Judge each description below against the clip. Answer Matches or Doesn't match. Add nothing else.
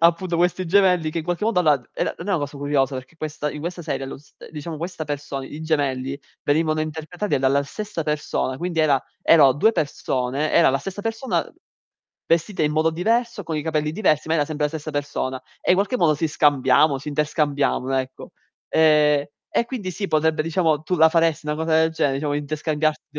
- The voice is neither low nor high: Matches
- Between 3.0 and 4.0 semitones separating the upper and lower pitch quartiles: Doesn't match